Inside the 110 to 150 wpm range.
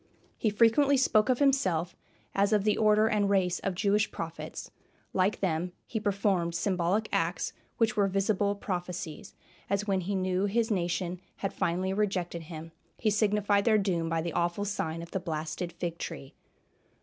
No: average, 165 wpm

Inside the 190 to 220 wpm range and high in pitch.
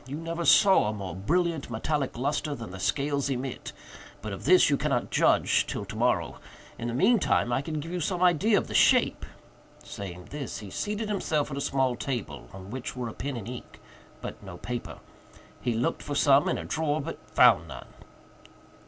No: average, 195 wpm; low, 135 Hz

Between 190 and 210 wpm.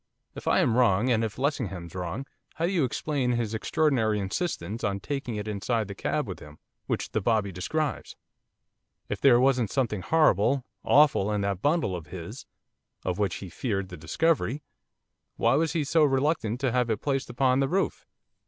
No: average, 180 wpm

